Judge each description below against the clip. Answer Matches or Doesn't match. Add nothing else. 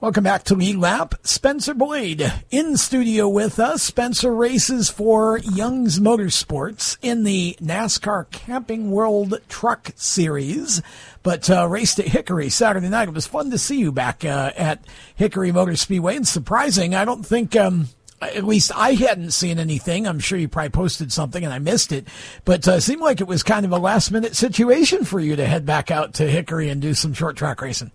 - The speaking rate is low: Doesn't match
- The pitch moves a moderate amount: Doesn't match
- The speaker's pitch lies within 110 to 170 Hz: Doesn't match